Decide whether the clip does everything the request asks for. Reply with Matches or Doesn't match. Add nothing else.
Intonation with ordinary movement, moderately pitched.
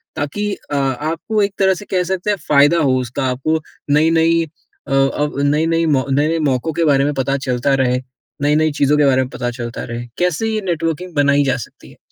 Matches